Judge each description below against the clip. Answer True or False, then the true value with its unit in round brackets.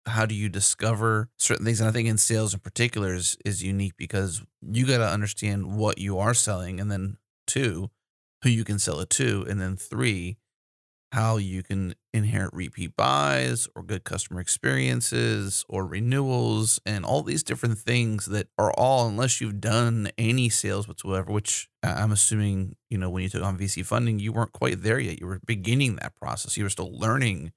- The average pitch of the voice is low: True (105 Hz)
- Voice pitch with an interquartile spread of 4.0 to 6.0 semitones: False (3.1 semitones)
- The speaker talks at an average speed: True (190 wpm)